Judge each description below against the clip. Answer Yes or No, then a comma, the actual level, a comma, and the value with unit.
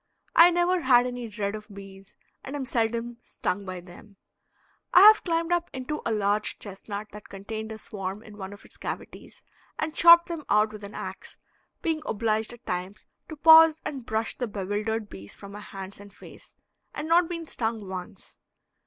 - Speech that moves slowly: No, average, 185 wpm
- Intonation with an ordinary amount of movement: No, wide, 6.9 semitones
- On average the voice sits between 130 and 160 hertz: No, high, 220 Hz